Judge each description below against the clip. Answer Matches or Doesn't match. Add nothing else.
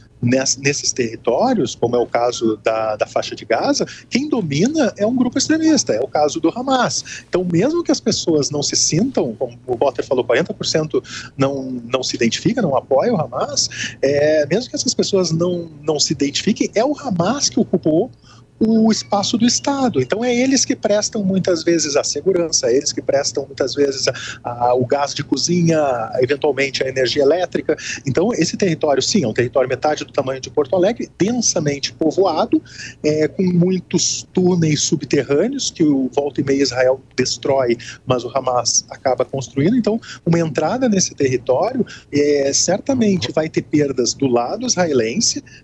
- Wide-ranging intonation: Matches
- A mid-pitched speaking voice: Matches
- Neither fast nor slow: Matches